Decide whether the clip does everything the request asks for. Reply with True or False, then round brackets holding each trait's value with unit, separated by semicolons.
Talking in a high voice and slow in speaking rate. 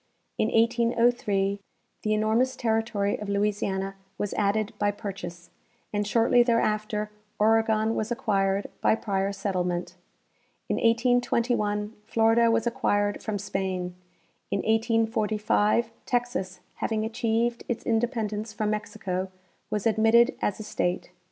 True (215 Hz; 120 wpm)